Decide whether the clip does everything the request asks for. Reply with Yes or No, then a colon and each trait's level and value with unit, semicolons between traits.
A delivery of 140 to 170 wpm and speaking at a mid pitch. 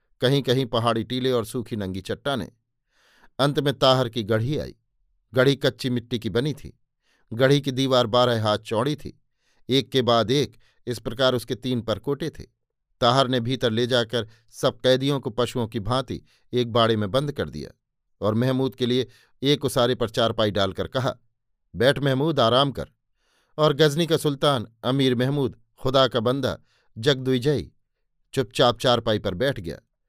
No: average, 165 wpm; low, 125 Hz